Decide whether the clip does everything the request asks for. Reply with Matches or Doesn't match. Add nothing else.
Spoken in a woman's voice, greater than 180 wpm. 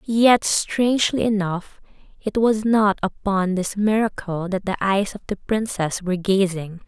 Doesn't match